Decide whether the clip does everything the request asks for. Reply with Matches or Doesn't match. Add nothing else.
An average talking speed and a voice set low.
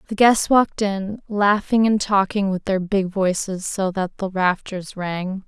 Doesn't match